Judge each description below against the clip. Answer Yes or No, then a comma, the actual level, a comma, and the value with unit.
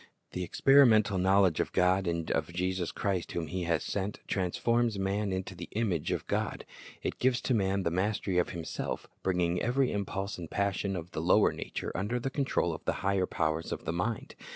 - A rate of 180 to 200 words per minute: Yes, average, 195 wpm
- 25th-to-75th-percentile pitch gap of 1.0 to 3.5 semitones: Yes, average, 2.9 semitones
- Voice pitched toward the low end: Yes, very low, 95 Hz